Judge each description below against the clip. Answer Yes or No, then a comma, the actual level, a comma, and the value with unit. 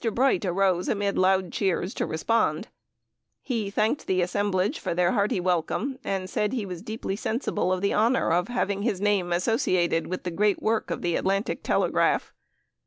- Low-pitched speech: No, high, 195 Hz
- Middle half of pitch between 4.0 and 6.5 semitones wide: No, average, 3.0 semitones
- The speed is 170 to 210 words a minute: Yes, average, 175 wpm